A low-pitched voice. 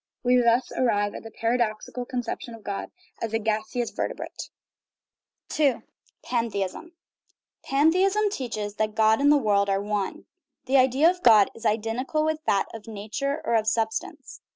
No: high, 230 Hz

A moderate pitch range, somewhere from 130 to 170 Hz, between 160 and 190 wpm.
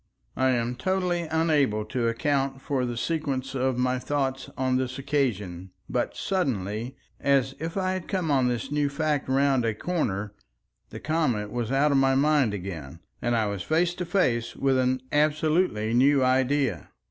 Yes: average, 4.0 semitones; low, 135 Hz; average, 170 wpm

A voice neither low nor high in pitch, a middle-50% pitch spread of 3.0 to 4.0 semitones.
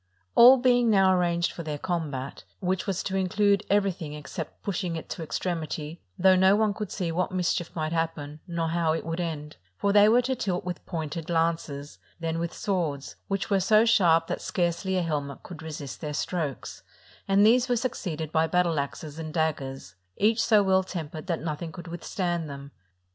Yes: medium, 170 Hz; average, 3.4 semitones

